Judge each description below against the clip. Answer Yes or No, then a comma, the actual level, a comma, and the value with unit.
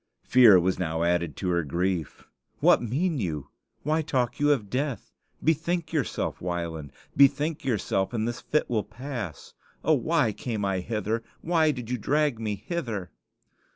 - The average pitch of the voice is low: Yes, low, 115 Hz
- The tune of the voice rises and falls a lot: Yes, wide, 7.8 semitones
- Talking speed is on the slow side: No, average, 155 wpm